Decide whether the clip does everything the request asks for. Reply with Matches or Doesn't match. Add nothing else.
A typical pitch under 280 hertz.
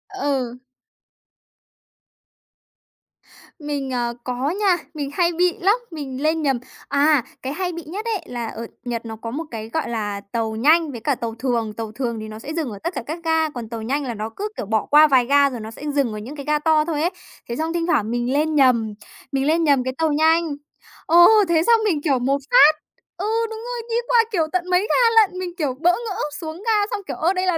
Doesn't match